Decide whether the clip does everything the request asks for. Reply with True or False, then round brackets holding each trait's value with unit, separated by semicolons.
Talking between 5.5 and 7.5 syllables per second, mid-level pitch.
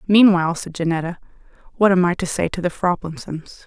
True (5.8 syllables/s; 180 Hz)